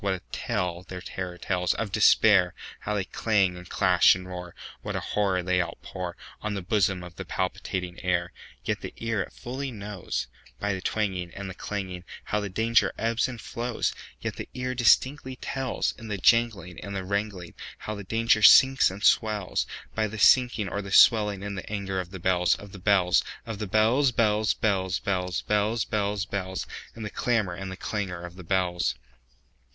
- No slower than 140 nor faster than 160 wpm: Yes, average, 155 wpm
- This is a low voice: Yes, low, 100 Hz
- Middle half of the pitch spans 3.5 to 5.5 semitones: No, average, 3.0 semitones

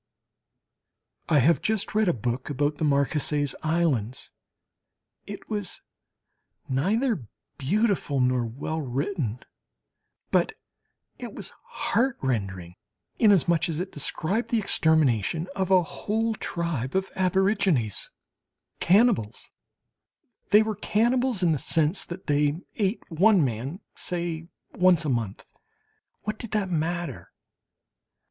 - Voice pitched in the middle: Yes, medium, 165 Hz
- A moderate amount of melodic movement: No, wide, 6.4 semitones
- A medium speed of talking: No, slow, 110 wpm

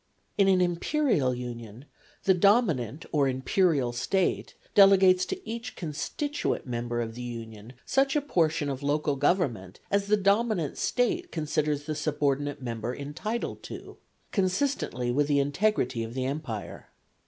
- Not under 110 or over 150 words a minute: Yes, average, 140 wpm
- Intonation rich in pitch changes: Yes, wide, 7.8 semitones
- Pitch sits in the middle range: Yes, medium, 150 Hz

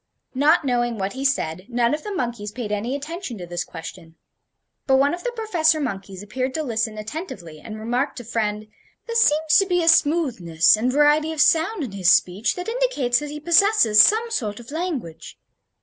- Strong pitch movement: Yes, wide, 7.1 semitones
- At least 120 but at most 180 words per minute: No, average, 195 wpm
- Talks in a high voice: Yes, very high, 255 Hz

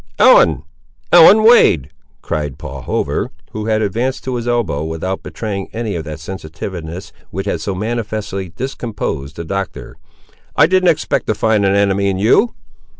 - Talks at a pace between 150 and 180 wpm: Yes, average, 155 wpm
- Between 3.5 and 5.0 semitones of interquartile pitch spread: No, wide, 5.5 semitones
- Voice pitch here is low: Yes, low, 100 Hz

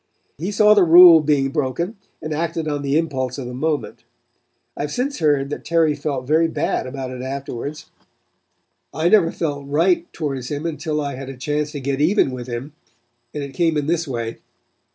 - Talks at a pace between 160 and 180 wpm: No, average, 195 wpm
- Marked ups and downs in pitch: No, average, 3.3 semitones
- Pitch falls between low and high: Yes, medium, 150 Hz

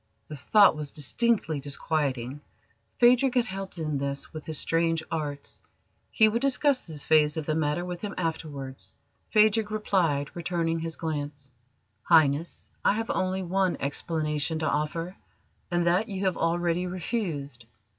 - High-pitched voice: No, medium, 165 Hz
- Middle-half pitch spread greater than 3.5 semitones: Yes, average, 4.2 semitones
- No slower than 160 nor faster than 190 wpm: No, average, 145 wpm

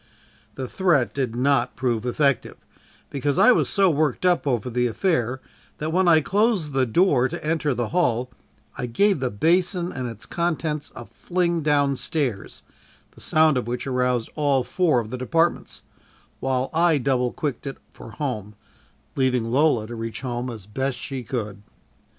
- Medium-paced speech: Yes, average, 170 wpm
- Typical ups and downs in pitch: Yes, average, 4.5 semitones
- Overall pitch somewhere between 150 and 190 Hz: No, low, 135 Hz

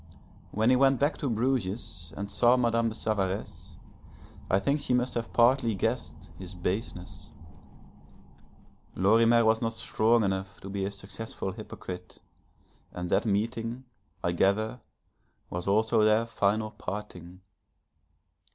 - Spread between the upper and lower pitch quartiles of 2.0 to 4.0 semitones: Yes, average, 3.2 semitones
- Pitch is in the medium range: No, low, 110 Hz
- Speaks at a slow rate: Yes, slow, 130 wpm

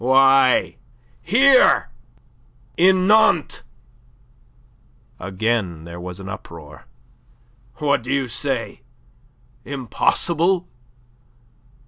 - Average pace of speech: No, slow, 65 wpm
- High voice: No, low, 135 Hz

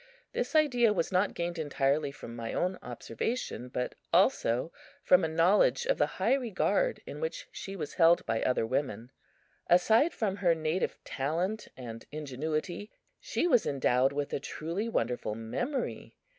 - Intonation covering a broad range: Yes, wide, 7.9 semitones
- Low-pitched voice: No, medium, 165 Hz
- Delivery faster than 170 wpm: No, average, 155 wpm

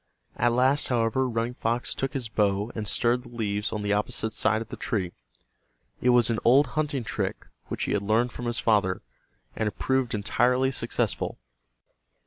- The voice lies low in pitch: Yes, low, 115 Hz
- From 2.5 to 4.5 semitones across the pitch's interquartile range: Yes, average, 2.8 semitones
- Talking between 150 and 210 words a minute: Yes, average, 180 wpm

